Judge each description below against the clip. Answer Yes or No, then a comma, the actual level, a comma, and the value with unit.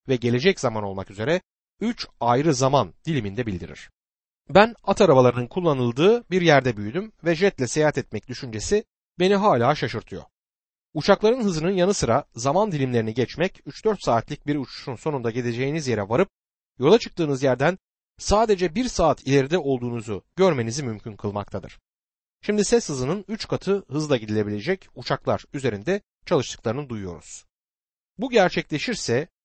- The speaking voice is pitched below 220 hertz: Yes, medium, 140 Hz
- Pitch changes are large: Yes, wide, 7.8 semitones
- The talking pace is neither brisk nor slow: Yes, average, 130 wpm